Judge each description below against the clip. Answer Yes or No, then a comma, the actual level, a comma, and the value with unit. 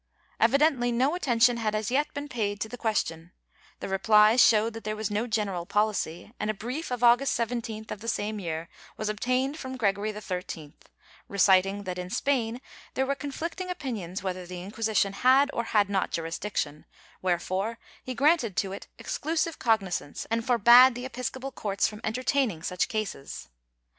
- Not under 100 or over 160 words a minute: No, average, 170 wpm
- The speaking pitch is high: Yes, high, 220 Hz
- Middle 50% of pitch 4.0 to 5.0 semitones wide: Yes, average, 4.3 semitones